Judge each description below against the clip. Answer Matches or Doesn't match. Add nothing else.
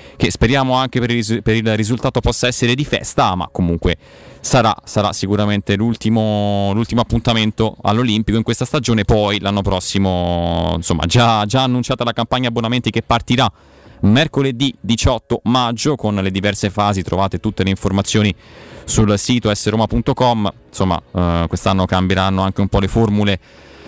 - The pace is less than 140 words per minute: Doesn't match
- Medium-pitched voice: Doesn't match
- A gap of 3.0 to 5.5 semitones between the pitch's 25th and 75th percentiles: Matches